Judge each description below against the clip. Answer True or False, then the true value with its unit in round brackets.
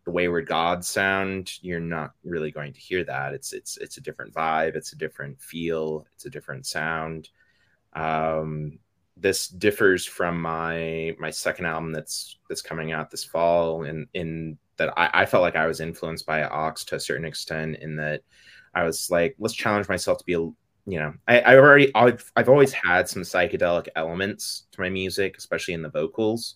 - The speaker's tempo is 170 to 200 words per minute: True (190 wpm)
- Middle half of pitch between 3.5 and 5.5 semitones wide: False (2.7 semitones)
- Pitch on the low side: True (80 Hz)